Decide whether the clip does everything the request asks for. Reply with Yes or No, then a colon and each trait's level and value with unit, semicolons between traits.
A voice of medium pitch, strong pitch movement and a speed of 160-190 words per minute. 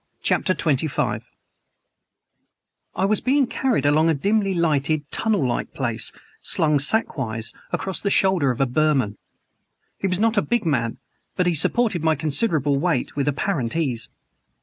No: medium, 155 Hz; wide, 6.1 semitones; average, 150 wpm